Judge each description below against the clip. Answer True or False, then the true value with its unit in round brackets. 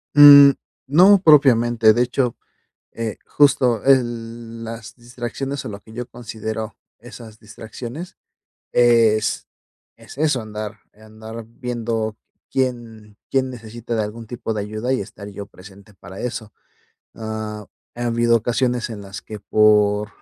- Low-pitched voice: True (115 Hz)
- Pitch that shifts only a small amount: True (2.2 semitones)